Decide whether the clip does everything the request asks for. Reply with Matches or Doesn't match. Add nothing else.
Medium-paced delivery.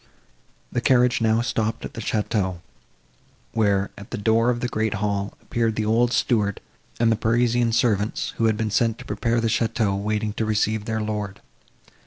Matches